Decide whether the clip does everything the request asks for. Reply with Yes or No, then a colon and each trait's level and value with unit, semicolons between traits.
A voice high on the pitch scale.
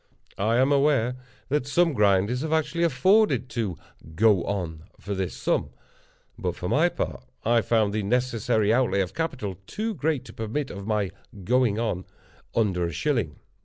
No: low, 115 Hz